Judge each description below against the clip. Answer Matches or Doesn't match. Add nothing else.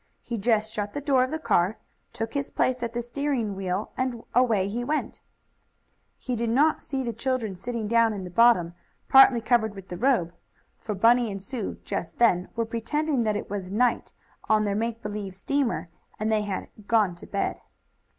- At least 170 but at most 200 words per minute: Matches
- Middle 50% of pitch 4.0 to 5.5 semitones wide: Doesn't match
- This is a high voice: Matches